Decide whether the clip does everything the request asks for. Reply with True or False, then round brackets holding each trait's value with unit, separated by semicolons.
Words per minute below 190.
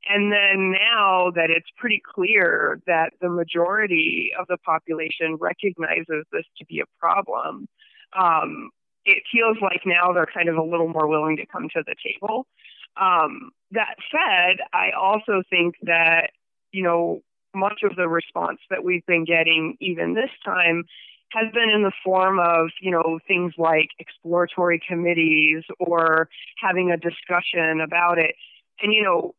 True (155 wpm)